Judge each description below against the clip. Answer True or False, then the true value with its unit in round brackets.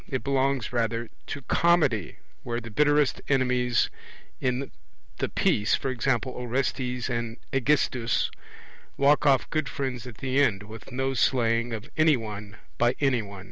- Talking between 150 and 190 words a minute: False (140 wpm)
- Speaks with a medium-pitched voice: False (125 Hz)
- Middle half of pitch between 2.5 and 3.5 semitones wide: True (2.9 semitones)